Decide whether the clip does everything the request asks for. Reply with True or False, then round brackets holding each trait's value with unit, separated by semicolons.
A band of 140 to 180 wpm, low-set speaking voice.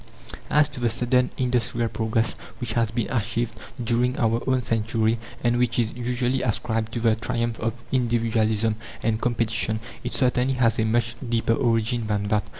True (165 wpm; 115 Hz)